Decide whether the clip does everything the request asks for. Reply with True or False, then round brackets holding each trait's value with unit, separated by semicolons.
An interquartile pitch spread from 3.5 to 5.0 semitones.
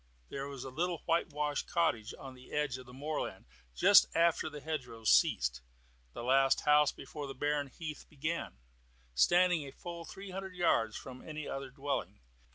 True (3.9 semitones)